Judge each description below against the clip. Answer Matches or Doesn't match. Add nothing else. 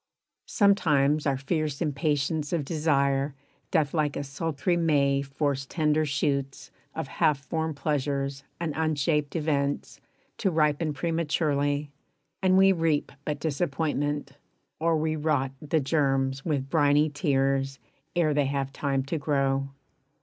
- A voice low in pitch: Doesn't match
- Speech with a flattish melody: Matches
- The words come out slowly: Matches